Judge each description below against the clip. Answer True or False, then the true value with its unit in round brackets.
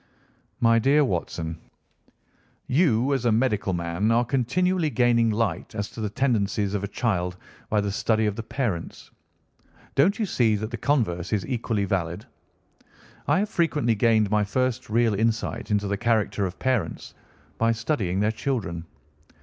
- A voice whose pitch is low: True (110 Hz)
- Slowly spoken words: False (160 wpm)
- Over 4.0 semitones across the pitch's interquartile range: False (3.7 semitones)